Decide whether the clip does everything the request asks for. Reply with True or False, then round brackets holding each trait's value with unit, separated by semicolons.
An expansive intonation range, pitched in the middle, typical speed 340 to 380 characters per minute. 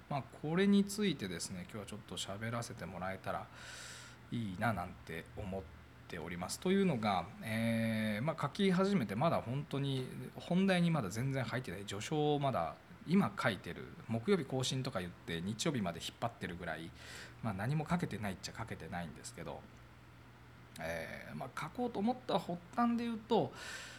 False (9.0 semitones; 120 Hz; 360 characters per minute)